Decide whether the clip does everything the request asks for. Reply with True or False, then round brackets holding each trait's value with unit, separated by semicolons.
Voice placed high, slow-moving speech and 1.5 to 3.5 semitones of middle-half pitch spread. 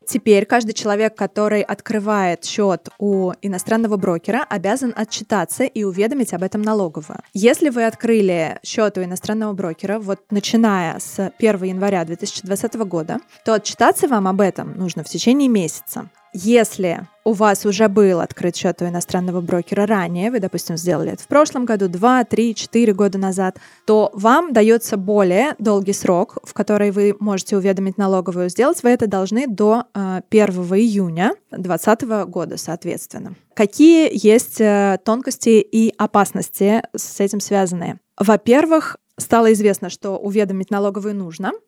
False (205 Hz; 145 wpm; 2.8 semitones)